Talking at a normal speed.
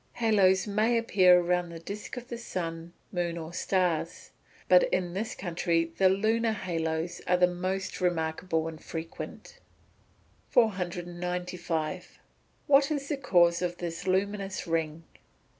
No: slow, 130 wpm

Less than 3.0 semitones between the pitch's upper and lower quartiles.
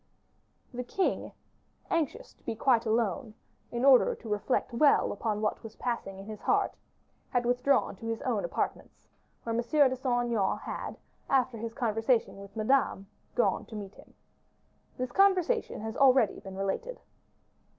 No: average, 3.5 semitones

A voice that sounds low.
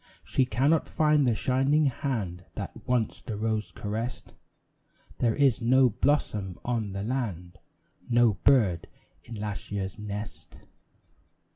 Yes: low, 115 Hz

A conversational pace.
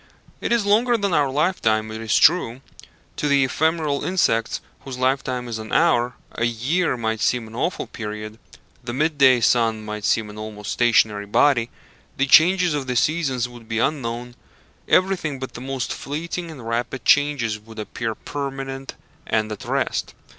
Yes: average, 170 wpm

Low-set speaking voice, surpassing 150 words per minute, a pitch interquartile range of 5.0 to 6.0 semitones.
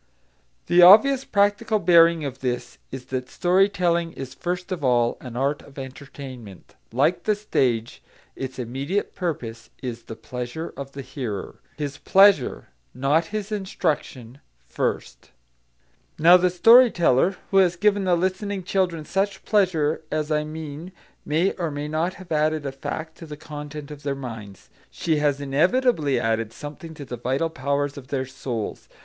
No: medium, 150 Hz; average, 160 wpm; average, 5.3 semitones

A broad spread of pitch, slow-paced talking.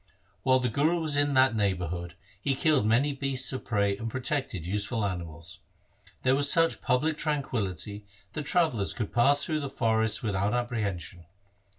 No: wide, 5.8 semitones; average, 165 wpm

